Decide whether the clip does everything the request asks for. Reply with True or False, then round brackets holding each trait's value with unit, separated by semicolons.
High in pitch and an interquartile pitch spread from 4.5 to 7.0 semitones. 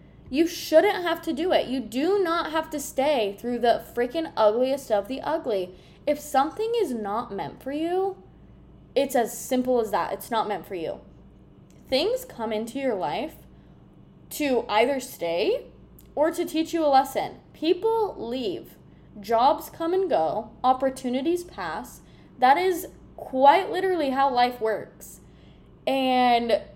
True (275 Hz; 5.4 semitones)